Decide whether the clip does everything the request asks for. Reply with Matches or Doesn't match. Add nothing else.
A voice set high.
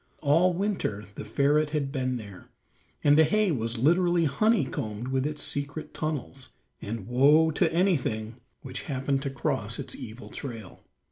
Doesn't match